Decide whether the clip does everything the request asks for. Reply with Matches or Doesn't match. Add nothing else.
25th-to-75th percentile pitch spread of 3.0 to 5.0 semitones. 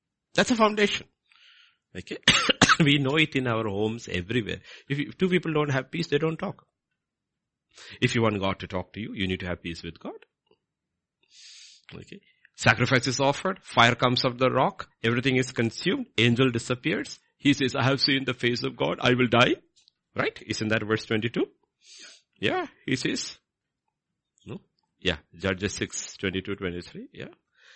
Matches